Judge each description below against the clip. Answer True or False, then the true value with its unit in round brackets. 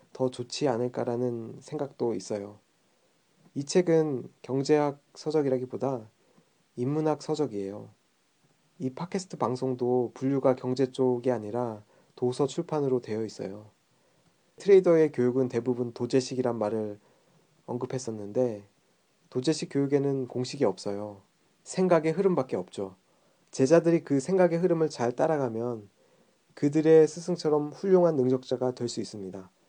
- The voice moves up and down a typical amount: True (4.3 semitones)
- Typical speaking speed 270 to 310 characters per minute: True (295 characters per minute)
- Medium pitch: False (130 Hz)